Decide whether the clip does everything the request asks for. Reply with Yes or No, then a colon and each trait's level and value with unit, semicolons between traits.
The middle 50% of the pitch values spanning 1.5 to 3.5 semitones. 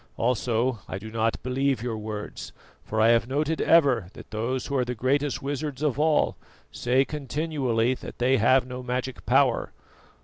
Yes: average, 3.2 semitones